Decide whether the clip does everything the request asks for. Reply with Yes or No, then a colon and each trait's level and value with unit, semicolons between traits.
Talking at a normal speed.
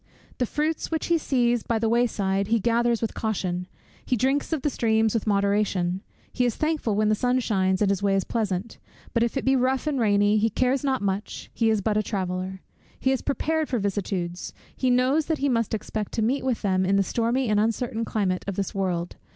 No: fast, 225 wpm